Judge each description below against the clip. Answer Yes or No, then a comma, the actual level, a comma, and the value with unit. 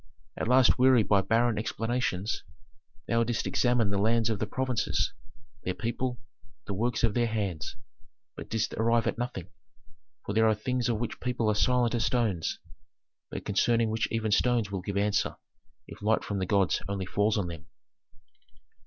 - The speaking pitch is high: No, low, 110 Hz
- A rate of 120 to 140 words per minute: No, average, 170 wpm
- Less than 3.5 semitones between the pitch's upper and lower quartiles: Yes, average, 2.8 semitones